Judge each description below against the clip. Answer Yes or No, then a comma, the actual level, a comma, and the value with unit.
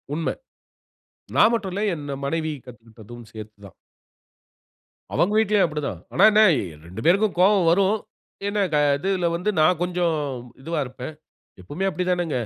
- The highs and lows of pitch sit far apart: Yes, wide, 6.7 semitones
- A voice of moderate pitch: Yes, medium, 170 Hz